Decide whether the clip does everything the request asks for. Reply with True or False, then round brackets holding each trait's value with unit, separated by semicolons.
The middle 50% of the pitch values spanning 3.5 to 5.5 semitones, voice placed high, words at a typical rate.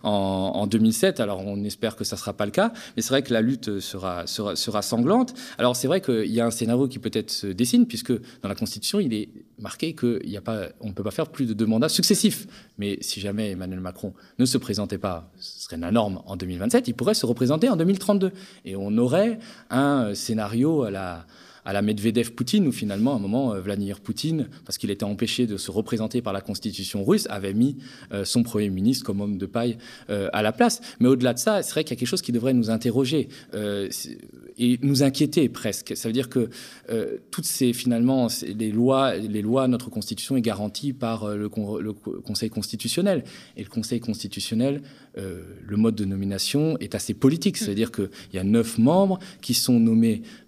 False (4.7 semitones; 115 Hz; 205 wpm)